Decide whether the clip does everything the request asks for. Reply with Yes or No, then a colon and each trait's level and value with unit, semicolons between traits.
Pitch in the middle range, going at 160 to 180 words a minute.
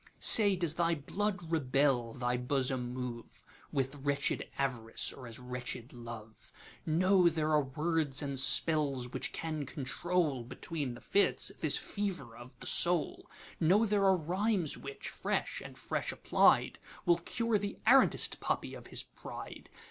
No: medium, 145 Hz; slow, 135 wpm